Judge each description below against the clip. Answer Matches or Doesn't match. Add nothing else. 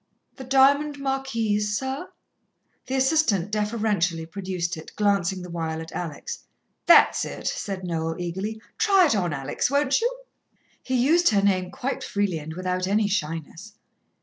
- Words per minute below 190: Matches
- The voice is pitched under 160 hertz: Doesn't match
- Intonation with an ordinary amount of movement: Doesn't match